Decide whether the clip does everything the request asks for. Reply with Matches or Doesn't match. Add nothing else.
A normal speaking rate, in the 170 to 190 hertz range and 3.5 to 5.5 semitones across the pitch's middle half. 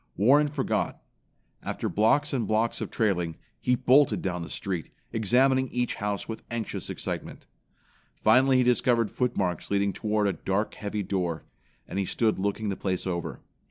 Doesn't match